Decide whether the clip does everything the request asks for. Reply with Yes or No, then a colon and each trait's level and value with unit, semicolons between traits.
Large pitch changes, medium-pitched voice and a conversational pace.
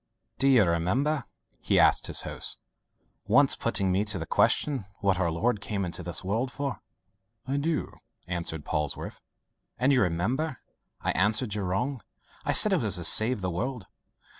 No: wide, 6.4 semitones; low, 105 Hz; average, 170 wpm